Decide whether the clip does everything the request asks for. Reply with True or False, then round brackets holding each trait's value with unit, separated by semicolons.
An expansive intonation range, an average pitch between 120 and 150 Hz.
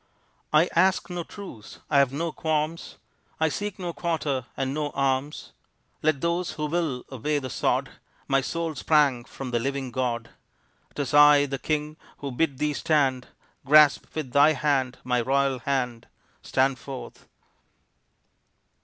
False (3.0 semitones; 140 Hz)